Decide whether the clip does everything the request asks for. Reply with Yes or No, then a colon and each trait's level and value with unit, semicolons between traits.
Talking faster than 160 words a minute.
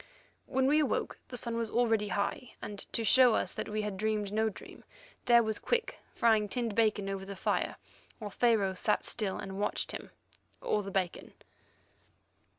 Yes: average, 170 wpm